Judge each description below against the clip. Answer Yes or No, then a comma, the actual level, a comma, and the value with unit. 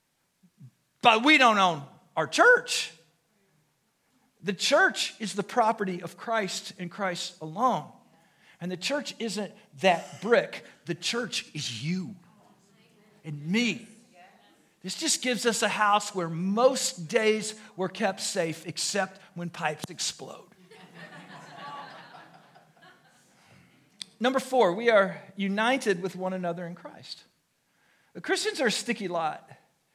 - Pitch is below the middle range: No, high, 200 Hz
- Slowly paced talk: Yes, slow, 120 wpm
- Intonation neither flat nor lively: Yes, average, 4.4 semitones